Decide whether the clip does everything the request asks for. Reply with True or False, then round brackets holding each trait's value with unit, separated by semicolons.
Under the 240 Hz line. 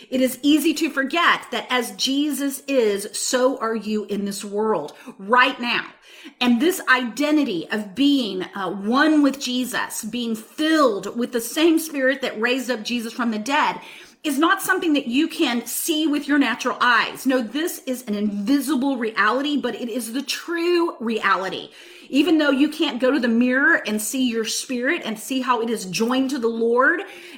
False (255 Hz)